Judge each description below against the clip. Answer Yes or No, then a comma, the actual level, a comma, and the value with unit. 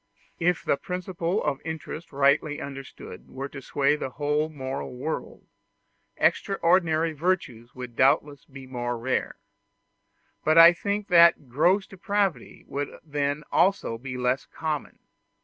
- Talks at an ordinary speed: No, slow, 130 wpm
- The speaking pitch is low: No, medium, 150 Hz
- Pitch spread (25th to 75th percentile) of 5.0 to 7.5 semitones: No, average, 4.0 semitones